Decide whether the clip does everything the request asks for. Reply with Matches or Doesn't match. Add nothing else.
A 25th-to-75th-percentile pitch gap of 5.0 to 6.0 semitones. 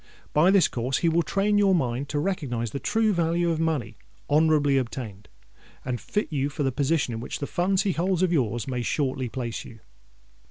Matches